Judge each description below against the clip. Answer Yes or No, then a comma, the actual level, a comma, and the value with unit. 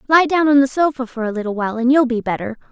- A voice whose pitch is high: Yes, very high, 255 Hz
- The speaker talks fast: Yes, fast, 290 wpm